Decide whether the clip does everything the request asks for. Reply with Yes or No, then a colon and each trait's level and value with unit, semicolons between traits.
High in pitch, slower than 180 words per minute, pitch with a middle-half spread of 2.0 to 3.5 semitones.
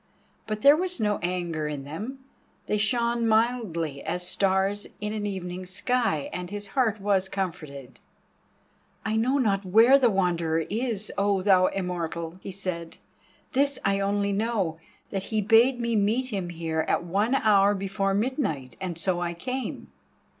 No: high, 200 Hz; average, 155 wpm; average, 4.1 semitones